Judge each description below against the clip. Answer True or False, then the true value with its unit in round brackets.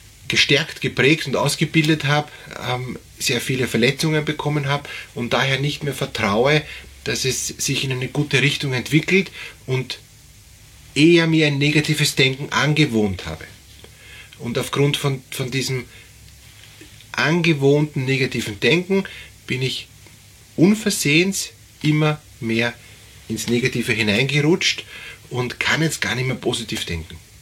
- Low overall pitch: True (130 Hz)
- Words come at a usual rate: False (120 wpm)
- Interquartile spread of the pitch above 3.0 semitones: True (4.7 semitones)